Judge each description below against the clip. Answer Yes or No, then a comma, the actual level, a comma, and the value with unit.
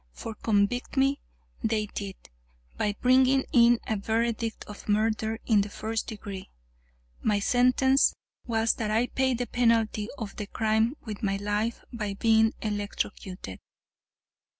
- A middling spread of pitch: No, narrow, 2.2 semitones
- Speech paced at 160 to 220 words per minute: No, slow, 135 wpm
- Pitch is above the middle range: Yes, high, 220 Hz